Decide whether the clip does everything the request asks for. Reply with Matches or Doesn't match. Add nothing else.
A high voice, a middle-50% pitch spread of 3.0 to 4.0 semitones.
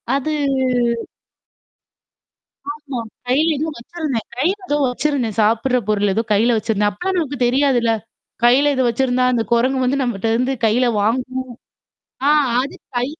Matches